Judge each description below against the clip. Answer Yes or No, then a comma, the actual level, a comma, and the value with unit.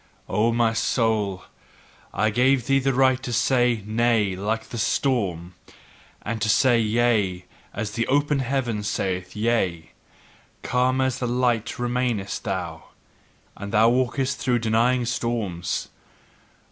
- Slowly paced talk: Yes, slow, 130 wpm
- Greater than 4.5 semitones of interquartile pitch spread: No, average, 3.1 semitones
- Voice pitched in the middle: No, low, 115 Hz